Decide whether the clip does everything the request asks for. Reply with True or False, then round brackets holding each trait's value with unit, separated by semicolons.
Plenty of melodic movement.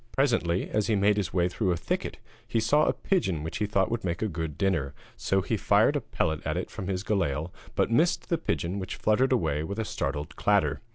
False (4.5 semitones)